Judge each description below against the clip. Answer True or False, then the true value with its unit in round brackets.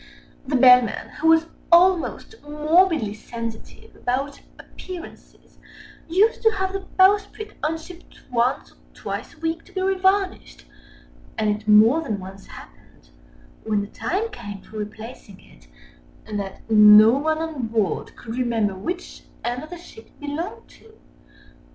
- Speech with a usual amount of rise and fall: False (8.5 semitones)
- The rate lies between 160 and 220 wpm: False (140 wpm)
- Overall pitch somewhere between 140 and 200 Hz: False (280 Hz)